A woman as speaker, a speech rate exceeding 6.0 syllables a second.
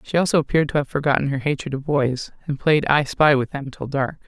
Yes: female; 6.2 syllables/s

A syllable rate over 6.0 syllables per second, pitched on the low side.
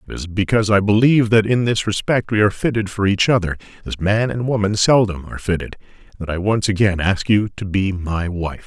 No: 5.8 syllables/s; low, 100 Hz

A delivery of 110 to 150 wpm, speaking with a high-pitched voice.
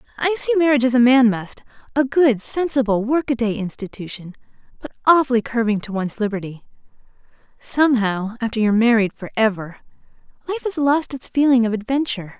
Yes: average, 145 wpm; high, 240 Hz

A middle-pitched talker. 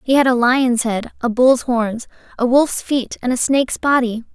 No: high, 245 Hz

